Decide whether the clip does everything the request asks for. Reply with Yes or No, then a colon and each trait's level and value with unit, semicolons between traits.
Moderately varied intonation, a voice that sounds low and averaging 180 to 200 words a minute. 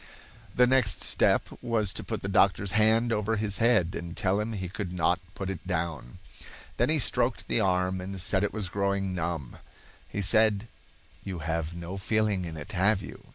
Yes: average, 3.3 semitones; very low, 95 Hz; average, 190 wpm